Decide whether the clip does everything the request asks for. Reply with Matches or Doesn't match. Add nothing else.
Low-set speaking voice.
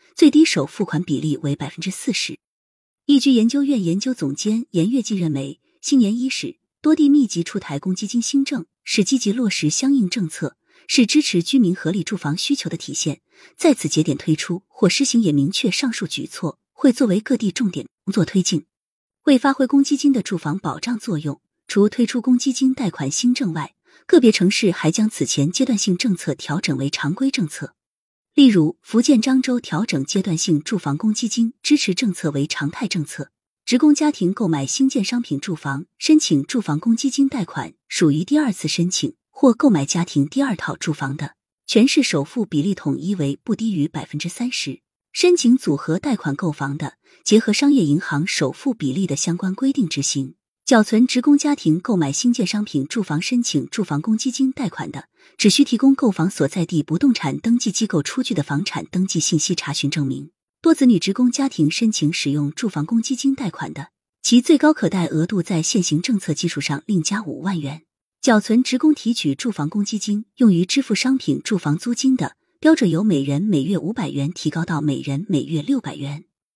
Doesn't match